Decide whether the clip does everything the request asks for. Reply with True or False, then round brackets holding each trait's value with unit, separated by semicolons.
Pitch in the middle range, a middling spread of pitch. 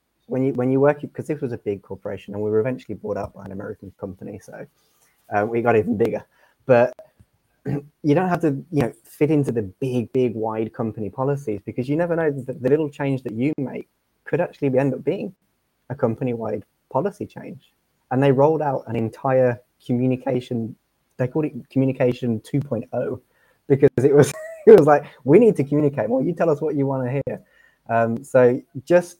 False (130 Hz; 3.8 semitones)